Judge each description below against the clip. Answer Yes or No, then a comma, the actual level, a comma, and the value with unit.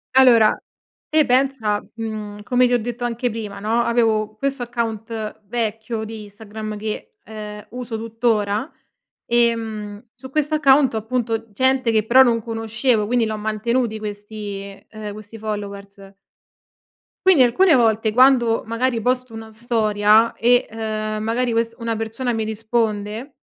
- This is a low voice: No, high, 225 Hz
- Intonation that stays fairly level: Yes, narrow, 2.2 semitones